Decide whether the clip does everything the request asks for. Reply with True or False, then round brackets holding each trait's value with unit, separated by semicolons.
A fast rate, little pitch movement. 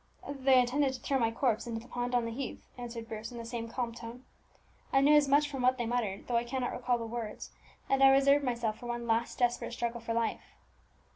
True (235 wpm; 2.3 semitones)